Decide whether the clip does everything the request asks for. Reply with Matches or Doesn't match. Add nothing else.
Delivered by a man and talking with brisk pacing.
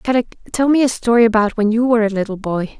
Doesn't match